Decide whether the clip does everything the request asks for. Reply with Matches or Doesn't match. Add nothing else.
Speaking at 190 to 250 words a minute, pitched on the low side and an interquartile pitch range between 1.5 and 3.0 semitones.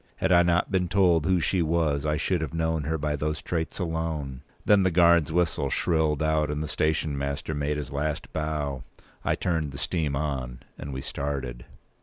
Matches